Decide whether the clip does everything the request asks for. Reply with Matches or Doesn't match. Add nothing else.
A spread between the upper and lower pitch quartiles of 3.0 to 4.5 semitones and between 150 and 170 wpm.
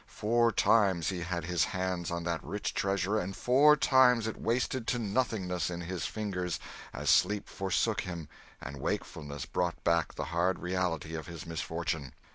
Matches